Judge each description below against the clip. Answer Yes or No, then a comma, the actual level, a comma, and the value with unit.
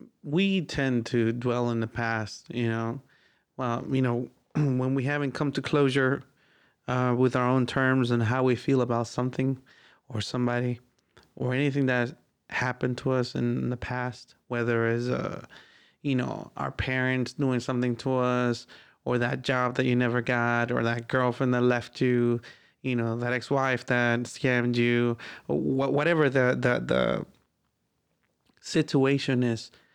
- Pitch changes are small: Yes, narrow, 1.8 semitones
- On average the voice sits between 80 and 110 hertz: No, low, 125 Hz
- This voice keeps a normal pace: Yes, average, 160 wpm